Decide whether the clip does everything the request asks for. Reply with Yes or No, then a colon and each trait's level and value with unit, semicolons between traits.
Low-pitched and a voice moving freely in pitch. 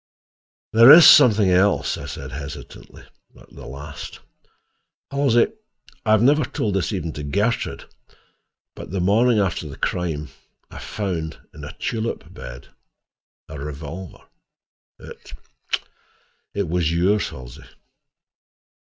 Yes: very low, 90 Hz; wide, 6.3 semitones